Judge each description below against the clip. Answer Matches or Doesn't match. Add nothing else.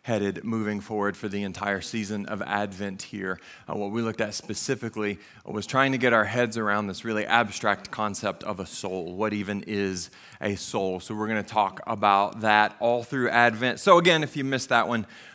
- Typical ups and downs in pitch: Doesn't match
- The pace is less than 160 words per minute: Doesn't match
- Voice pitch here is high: Doesn't match